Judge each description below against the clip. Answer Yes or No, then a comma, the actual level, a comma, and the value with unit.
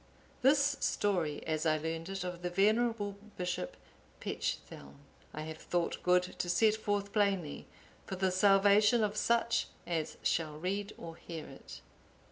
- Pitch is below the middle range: No, high, 190 Hz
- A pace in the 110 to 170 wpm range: Yes, average, 150 wpm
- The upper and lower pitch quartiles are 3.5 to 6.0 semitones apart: Yes, average, 3.9 semitones